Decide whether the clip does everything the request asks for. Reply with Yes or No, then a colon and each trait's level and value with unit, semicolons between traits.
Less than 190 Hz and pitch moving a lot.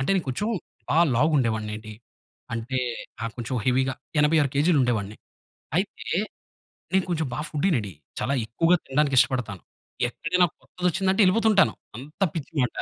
Yes: medium, 140 Hz; wide, 5.8 semitones